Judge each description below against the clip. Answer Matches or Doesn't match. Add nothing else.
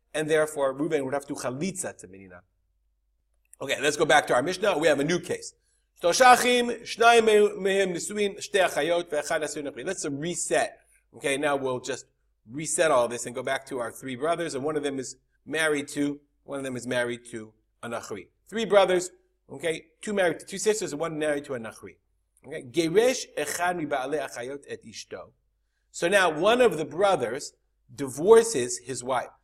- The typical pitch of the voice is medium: Matches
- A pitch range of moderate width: Doesn't match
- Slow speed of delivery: Doesn't match